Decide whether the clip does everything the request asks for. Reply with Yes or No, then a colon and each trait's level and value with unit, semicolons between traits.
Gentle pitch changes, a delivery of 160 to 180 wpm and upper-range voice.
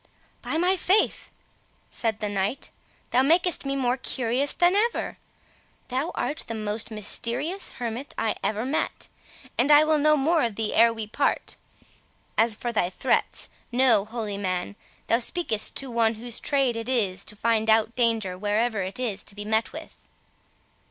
No: average, 4.2 semitones; average, 165 wpm; high, 230 Hz